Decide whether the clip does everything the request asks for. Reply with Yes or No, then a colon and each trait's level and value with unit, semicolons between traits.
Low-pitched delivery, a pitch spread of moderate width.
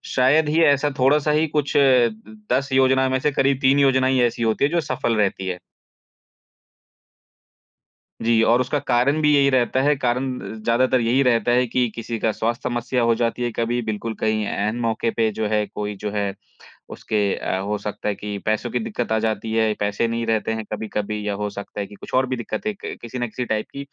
Yes: low, 120 Hz; average, 3.3 semitones